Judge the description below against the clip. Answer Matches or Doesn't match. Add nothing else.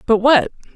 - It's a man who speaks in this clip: Doesn't match